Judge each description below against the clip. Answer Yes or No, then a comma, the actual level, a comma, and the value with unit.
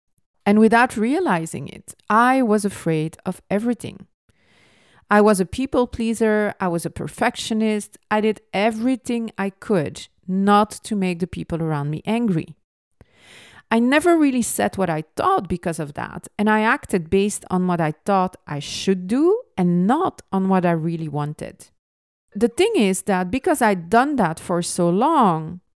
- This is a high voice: Yes, high, 195 Hz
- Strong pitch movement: No, average, 4.7 semitones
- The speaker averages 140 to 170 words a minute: Yes, average, 165 wpm